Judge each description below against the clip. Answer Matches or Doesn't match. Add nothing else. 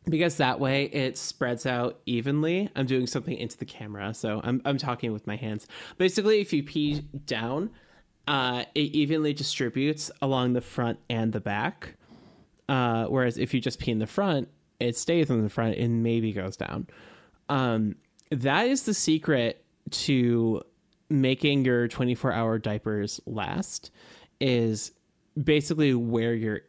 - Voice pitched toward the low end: Matches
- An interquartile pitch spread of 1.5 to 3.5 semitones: Doesn't match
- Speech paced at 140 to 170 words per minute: Matches